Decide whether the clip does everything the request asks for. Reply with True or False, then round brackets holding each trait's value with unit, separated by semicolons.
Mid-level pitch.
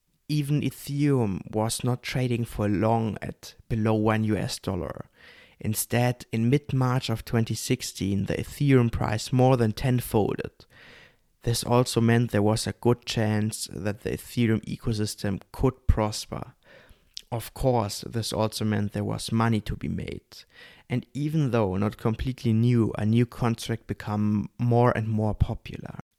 False (115 Hz)